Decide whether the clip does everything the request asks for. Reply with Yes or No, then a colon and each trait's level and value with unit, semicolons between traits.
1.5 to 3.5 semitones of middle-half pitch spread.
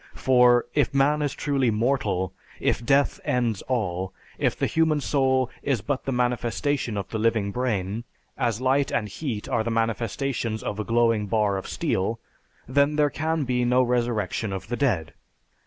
No: average, 4.0 semitones